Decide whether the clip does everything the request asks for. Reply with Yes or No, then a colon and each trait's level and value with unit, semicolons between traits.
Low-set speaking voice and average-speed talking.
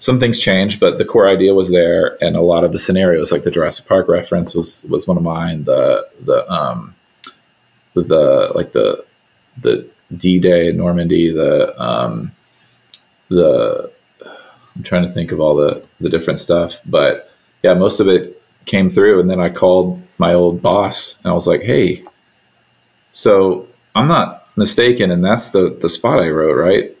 Yes: very low, 95 Hz; average, 180 wpm